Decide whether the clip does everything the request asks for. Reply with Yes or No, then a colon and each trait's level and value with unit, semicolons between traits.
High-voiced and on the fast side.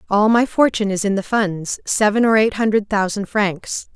No: high, 210 Hz; average, 195 wpm